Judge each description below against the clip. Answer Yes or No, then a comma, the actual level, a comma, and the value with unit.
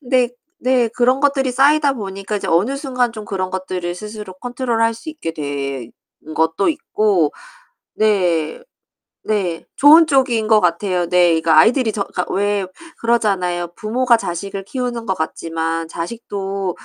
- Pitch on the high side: Yes, high, 205 Hz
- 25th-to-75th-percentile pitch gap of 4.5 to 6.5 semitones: Yes, wide, 5.6 semitones